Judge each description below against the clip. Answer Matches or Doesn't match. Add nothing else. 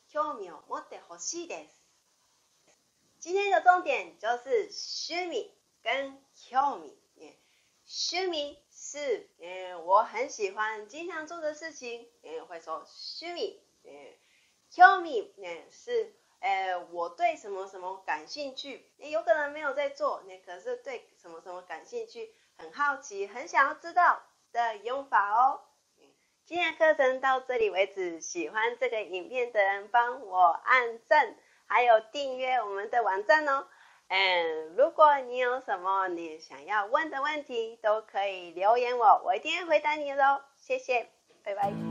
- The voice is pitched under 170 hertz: Doesn't match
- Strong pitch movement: Matches